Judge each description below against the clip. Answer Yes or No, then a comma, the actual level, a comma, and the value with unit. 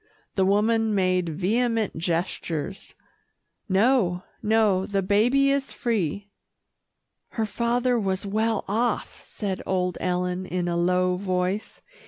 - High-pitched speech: Yes, high, 195 Hz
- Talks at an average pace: No, slow, 115 wpm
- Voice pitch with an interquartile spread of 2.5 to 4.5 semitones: Yes, average, 3.5 semitones